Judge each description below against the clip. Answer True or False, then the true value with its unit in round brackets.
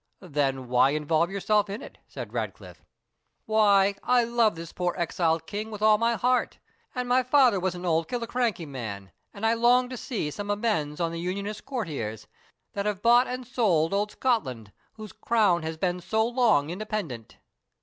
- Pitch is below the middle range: False (200 Hz)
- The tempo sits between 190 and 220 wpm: False (175 wpm)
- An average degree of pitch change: False (6.0 semitones)